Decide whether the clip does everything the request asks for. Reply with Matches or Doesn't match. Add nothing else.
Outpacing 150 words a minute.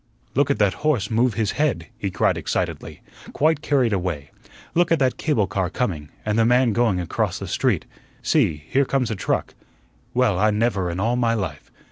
Matches